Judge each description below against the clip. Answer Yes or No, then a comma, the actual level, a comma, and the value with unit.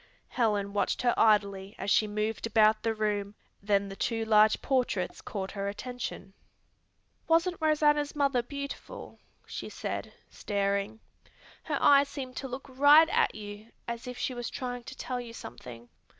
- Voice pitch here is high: Yes, high, 225 Hz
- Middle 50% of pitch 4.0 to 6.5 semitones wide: Yes, average, 4.5 semitones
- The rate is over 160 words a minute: No, average, 155 wpm